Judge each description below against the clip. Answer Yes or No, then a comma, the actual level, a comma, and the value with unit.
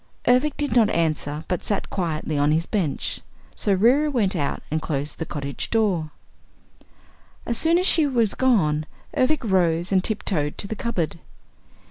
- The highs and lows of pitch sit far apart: Yes, wide, 7.2 semitones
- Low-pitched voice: No, high, 190 Hz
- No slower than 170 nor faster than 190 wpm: No, average, 160 wpm